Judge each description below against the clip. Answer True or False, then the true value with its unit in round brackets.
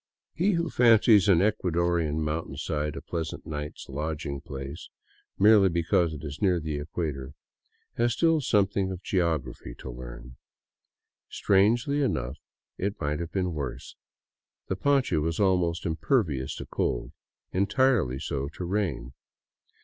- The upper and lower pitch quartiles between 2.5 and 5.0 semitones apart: False (5.5 semitones)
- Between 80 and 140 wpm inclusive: True (135 wpm)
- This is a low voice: True (85 Hz)